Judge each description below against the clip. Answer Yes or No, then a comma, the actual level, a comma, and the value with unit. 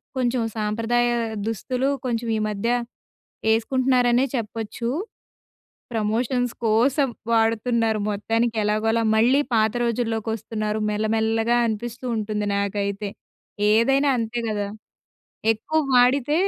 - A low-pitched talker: No, high, 225 Hz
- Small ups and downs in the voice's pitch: Yes, narrow, 2.1 semitones